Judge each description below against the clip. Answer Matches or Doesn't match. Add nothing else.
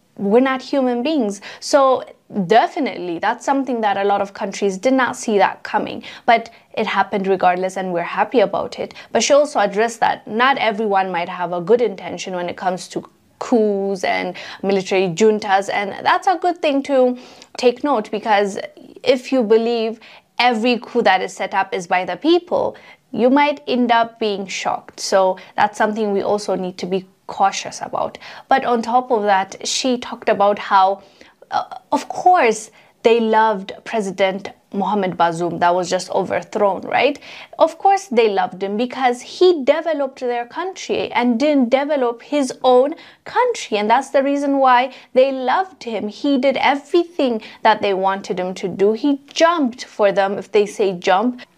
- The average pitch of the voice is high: Matches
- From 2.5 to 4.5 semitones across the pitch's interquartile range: Doesn't match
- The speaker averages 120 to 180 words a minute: Matches